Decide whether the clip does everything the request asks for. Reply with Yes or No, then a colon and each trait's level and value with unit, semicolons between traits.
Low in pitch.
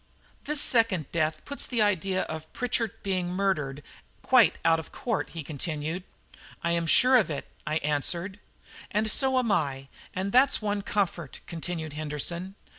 No: medium, 180 Hz